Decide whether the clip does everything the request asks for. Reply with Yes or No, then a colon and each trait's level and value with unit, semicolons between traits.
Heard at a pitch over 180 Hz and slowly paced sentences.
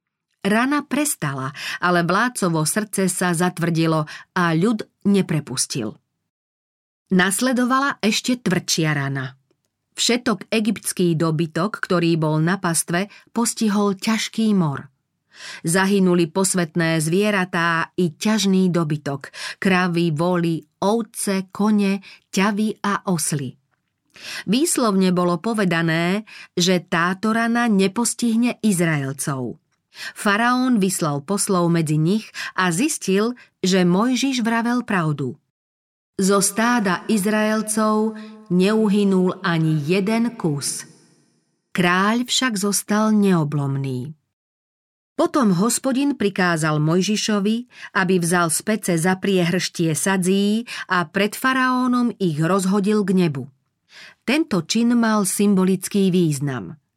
Yes: high, 190 Hz; slow, 95 wpm